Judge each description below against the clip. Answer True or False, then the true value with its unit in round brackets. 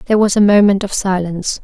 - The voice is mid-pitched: False (195 Hz)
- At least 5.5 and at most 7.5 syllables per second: True (6.3 syllables/s)